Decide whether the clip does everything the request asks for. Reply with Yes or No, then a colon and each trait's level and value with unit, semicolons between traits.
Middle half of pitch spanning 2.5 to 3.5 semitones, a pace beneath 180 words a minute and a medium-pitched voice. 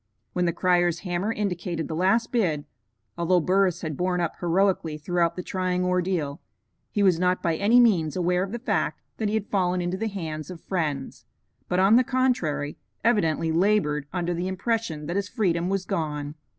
No: average, 3.0 semitones; average, 185 wpm; medium, 180 Hz